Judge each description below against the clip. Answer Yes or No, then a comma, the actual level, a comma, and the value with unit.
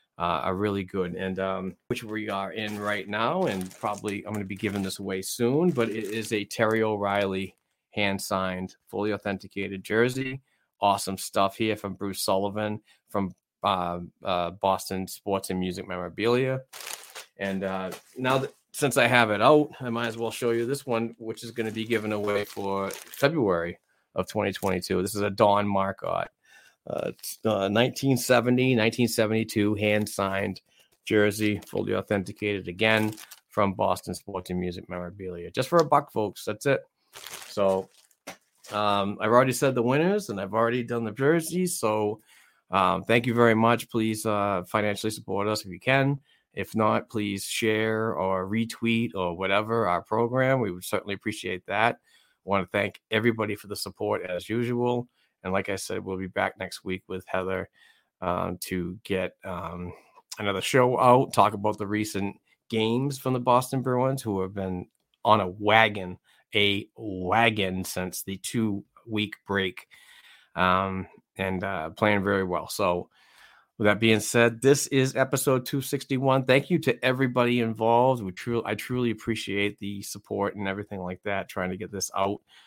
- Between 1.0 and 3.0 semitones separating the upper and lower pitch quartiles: No, average, 3.4 semitones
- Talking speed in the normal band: Yes, average, 165 wpm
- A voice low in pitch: Yes, low, 105 Hz